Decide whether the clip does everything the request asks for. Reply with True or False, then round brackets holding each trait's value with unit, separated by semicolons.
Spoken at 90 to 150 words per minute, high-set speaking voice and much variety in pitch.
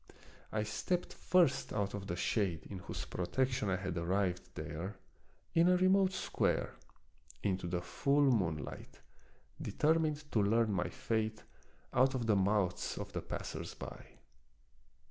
False (145 wpm; 105 Hz; 6.8 semitones)